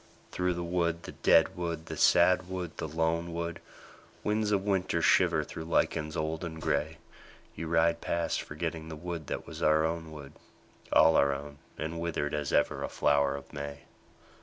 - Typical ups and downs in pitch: No, narrow, 1.8 semitones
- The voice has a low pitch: Yes, very low, 80 Hz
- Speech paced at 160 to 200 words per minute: Yes, average, 180 wpm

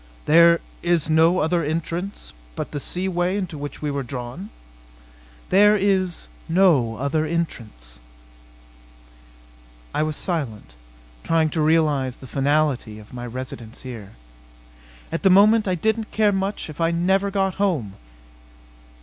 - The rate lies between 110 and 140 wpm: Yes, slow, 135 wpm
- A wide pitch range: Yes, wide, 5.9 semitones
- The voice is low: No, medium, 160 Hz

